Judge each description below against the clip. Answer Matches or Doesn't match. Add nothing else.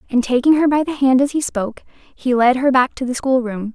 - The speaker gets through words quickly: Matches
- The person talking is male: Doesn't match